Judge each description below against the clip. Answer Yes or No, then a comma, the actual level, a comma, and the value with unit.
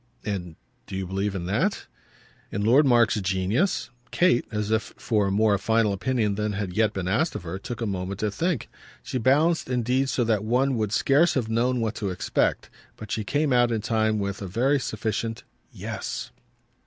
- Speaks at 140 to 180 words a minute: No, average, 190 wpm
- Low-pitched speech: Yes, low, 110 Hz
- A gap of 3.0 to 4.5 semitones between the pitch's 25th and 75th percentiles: Yes, average, 4.0 semitones